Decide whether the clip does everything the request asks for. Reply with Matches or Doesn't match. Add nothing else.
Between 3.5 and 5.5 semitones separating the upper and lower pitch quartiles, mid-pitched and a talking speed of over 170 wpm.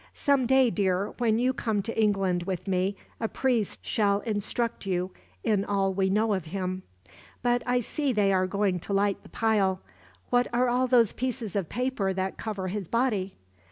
Doesn't match